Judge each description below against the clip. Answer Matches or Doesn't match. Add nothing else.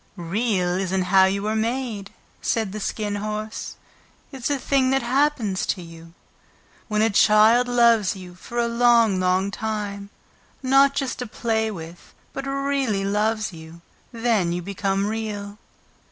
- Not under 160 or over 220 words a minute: Doesn't match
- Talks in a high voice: Matches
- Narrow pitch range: Doesn't match